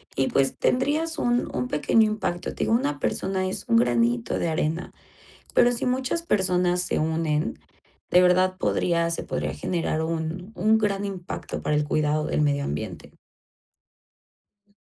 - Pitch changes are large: Yes, wide, 5.7 semitones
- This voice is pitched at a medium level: Yes, medium, 180 Hz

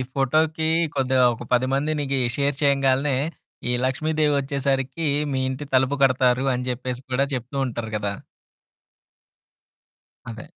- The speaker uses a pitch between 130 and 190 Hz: Yes, low, 135 Hz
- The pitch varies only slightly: Yes, narrow, 1.9 semitones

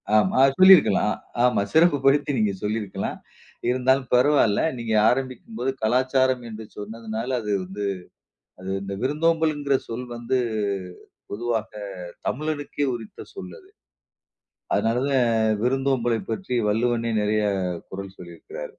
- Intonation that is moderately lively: Yes, average, 3.8 semitones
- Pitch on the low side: Yes, low, 120 Hz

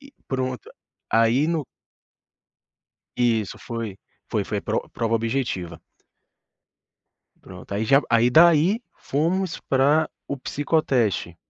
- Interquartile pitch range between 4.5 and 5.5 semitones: Yes, average, 5.2 semitones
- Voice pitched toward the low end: Yes, low, 130 Hz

